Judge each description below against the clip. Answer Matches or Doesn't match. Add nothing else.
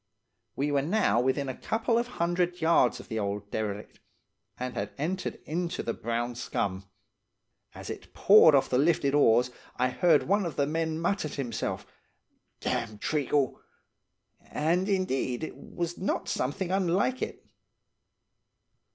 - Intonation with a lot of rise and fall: Matches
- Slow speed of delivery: Doesn't match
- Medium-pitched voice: Matches